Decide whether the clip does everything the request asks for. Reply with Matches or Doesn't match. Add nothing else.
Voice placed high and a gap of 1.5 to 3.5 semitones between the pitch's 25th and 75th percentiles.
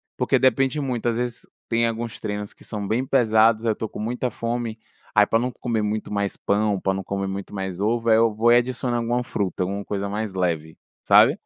Doesn't match